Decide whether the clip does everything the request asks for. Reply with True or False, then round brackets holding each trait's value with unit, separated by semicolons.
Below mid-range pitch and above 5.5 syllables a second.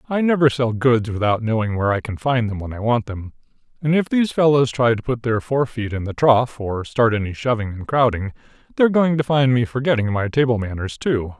True (120 Hz; 5.7 syllables/s)